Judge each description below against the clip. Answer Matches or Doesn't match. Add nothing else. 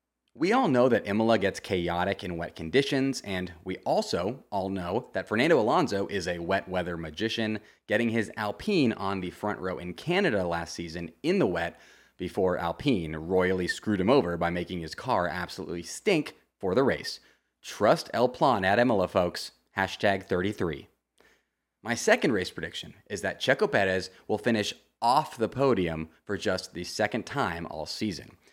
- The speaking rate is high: Doesn't match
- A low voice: Matches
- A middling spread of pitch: Matches